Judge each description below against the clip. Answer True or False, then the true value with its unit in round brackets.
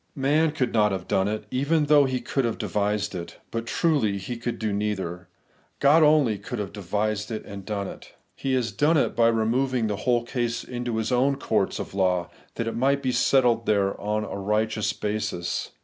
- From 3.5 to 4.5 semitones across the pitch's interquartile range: True (3.9 semitones)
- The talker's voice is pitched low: True (115 Hz)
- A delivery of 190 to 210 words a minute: True (195 wpm)